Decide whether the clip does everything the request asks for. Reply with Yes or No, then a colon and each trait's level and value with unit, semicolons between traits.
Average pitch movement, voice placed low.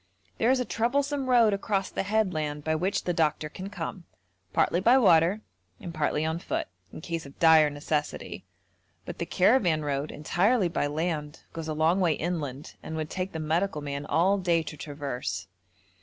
No: average, 4.3 semitones; medium, 165 Hz